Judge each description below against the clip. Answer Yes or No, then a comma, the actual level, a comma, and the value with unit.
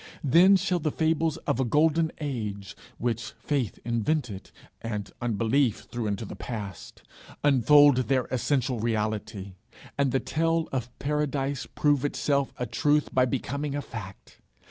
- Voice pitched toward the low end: Yes, low, 130 Hz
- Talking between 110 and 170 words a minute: Yes, average, 140 wpm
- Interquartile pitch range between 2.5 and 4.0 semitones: No, average, 4.5 semitones